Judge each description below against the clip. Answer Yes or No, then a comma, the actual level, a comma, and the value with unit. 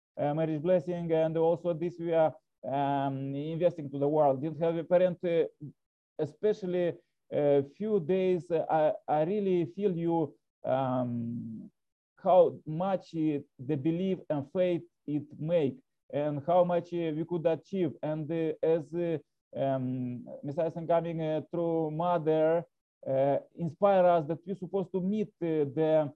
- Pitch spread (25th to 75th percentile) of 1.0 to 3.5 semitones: Yes, average, 2.9 semitones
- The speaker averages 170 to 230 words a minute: No, average, 150 wpm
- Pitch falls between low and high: Yes, medium, 165 Hz